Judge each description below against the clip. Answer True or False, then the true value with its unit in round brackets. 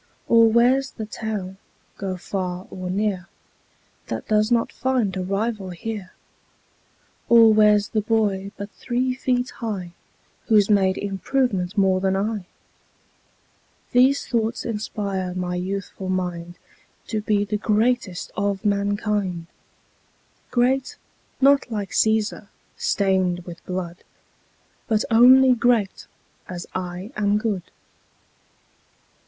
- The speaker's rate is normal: False (115 wpm)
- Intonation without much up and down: False (3.3 semitones)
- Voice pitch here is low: False (205 Hz)